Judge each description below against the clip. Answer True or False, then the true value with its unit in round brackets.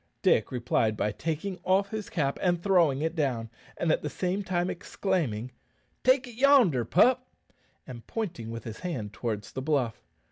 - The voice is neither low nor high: True (160 Hz)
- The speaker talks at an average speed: True (165 wpm)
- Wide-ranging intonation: True (8.3 semitones)